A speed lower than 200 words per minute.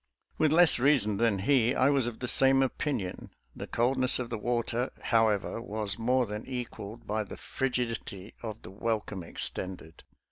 Yes: average, 165 wpm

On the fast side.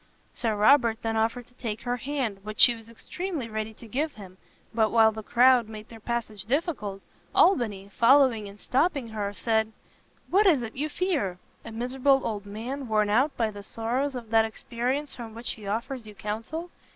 No: average, 190 wpm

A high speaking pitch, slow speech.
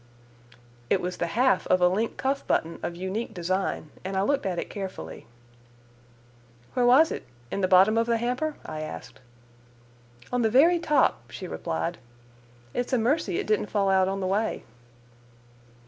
No: high, 195 Hz; average, 170 wpm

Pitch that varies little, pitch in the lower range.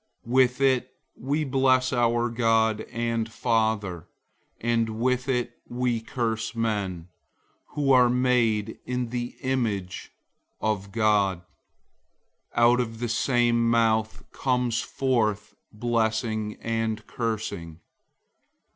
Yes: narrow, 2.1 semitones; low, 115 Hz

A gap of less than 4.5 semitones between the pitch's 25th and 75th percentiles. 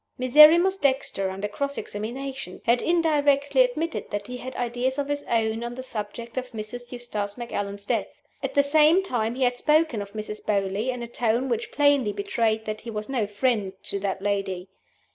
No: average, 4.9 semitones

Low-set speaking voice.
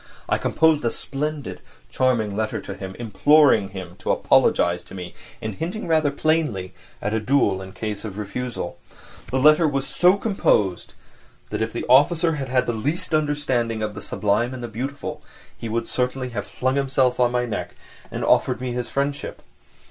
Yes: low, 125 Hz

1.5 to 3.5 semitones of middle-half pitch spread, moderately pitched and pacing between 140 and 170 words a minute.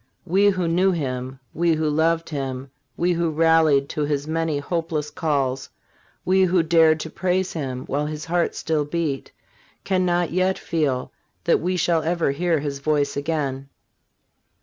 Yes: average, 3.1 semitones; medium, 160 Hz; average, 160 wpm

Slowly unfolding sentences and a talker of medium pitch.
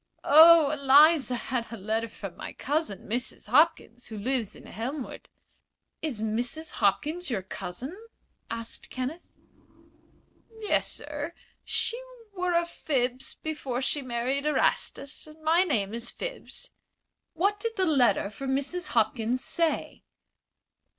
No: slow, 125 wpm; very high, 270 Hz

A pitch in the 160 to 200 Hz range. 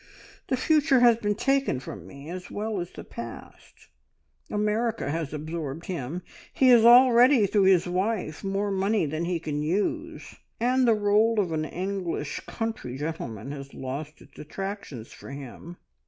Yes: high, 190 Hz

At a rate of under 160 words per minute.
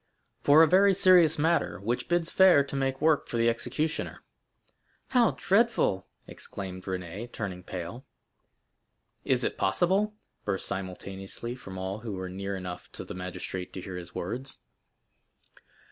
Yes: average, 145 wpm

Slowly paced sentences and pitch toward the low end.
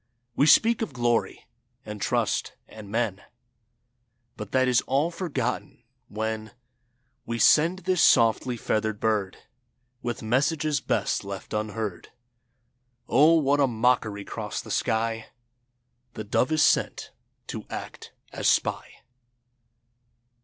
Yes: slow, 115 wpm; low, 120 Hz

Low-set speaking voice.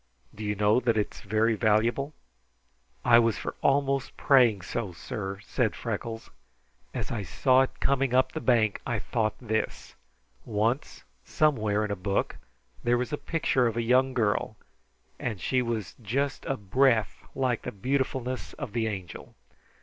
Yes: low, 115 Hz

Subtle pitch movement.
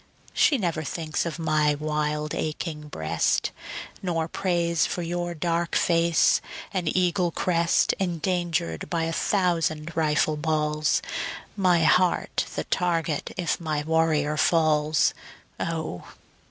Yes: narrow, 2.2 semitones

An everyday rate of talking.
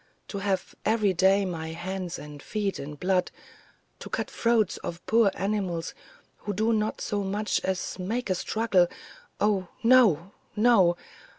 Yes: average, 155 wpm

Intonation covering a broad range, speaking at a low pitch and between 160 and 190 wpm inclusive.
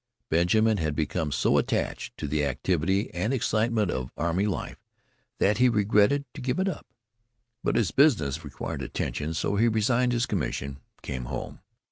Yes: wide, 7.0 semitones; low, 100 Hz; average, 165 wpm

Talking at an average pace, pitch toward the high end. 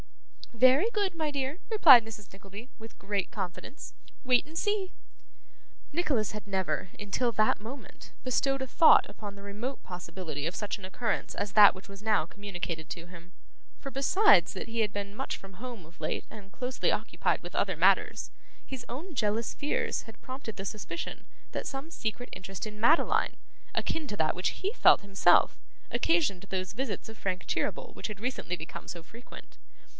Yes: average, 175 wpm; high, 215 Hz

